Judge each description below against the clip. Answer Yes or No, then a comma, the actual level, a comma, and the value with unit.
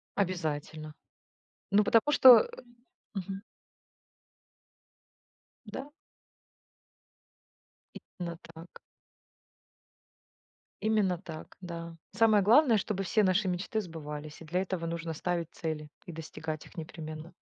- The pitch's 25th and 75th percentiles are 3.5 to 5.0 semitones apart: Yes, average, 3.9 semitones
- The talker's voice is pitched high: No, medium, 175 Hz